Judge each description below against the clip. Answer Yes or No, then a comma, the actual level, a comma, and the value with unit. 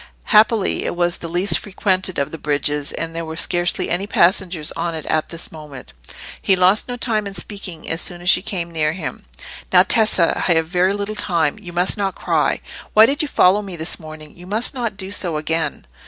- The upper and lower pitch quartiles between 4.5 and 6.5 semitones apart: No, average, 3.6 semitones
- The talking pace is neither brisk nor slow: No, fast, 215 wpm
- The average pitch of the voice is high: No, medium, 175 Hz